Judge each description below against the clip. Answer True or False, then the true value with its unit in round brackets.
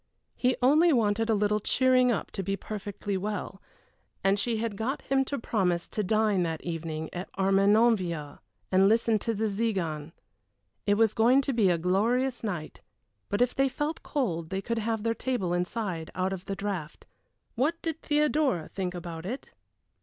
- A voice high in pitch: True (210 Hz)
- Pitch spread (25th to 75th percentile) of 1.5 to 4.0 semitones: False (4.5 semitones)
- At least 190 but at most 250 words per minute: False (175 wpm)